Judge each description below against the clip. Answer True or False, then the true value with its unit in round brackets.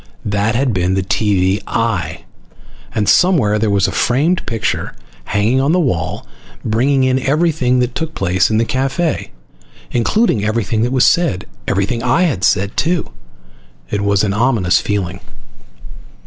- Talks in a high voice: False (115 Hz)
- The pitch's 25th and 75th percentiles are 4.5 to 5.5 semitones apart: True (4.9 semitones)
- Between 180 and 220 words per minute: False (150 wpm)